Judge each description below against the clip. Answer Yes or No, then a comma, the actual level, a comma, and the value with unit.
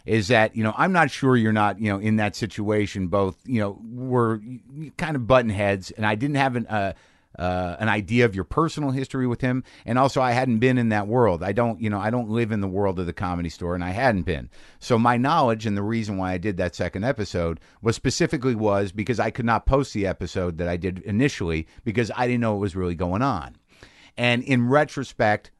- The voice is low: Yes, low, 110 Hz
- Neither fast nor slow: No, fast, 235 wpm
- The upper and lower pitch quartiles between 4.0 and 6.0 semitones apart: Yes, average, 4.3 semitones